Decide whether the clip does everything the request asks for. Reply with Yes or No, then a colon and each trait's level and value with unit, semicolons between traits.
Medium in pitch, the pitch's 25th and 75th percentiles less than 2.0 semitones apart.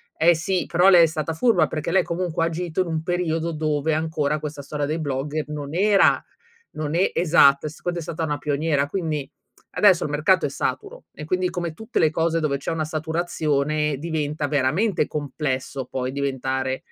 No: medium, 155 Hz; narrow, 2.6 semitones